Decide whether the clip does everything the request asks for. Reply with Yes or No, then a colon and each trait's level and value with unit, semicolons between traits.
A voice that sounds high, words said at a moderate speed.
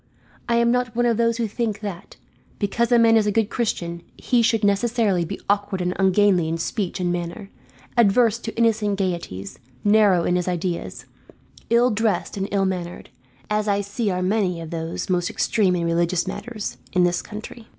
Yes: high, 200 Hz; average, 185 wpm